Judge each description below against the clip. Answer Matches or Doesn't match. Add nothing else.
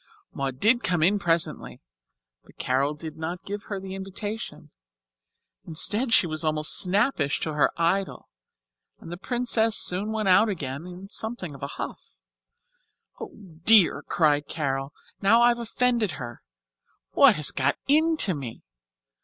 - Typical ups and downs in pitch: Doesn't match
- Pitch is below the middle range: Doesn't match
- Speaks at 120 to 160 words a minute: Matches